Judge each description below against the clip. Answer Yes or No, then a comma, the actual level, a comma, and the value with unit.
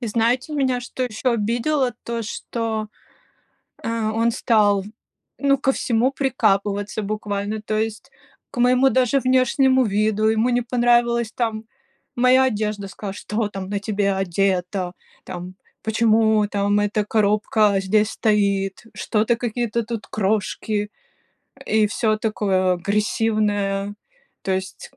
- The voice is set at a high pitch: Yes, high, 215 Hz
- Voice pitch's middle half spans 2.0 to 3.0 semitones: Yes, average, 2.7 semitones